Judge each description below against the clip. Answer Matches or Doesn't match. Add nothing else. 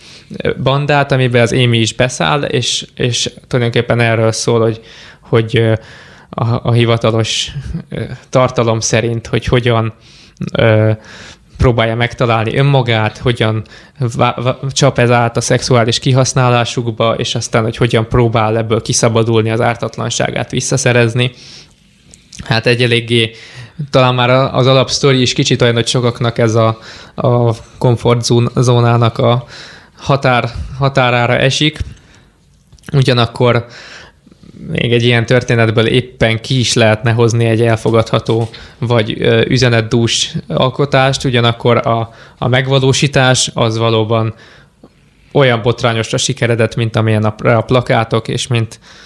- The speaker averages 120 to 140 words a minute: Doesn't match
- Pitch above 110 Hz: Matches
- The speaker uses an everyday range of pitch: Doesn't match